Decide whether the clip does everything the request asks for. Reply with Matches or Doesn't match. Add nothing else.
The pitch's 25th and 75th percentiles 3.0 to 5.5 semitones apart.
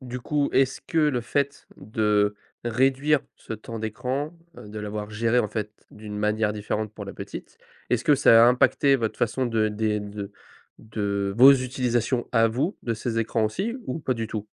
Matches